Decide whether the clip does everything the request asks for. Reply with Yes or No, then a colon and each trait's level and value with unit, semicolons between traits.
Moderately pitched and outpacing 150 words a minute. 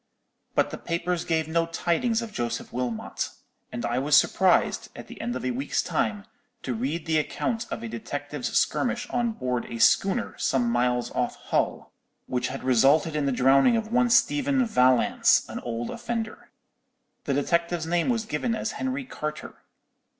Yes: medium, 155 Hz; average, 170 wpm